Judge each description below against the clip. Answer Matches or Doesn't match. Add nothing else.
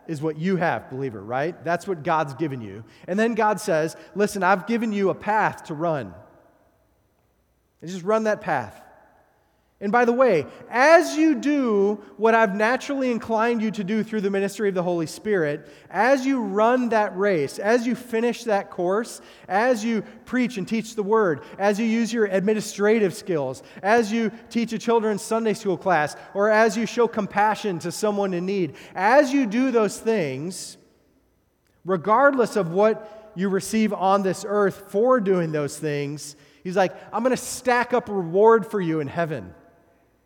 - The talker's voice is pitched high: Matches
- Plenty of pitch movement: Doesn't match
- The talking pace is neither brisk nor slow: Matches